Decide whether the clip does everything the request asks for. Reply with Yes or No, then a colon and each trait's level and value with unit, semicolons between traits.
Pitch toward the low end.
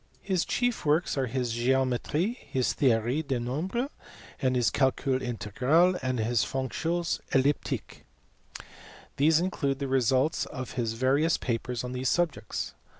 Yes: low, 130 Hz